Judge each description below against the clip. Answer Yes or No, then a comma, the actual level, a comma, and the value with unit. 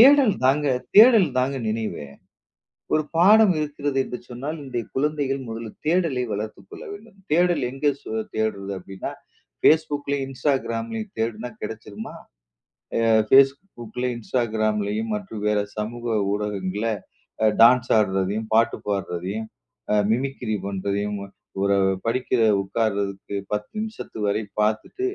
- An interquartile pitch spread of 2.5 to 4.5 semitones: No, average, 5.3 semitones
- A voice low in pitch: Yes, low, 115 Hz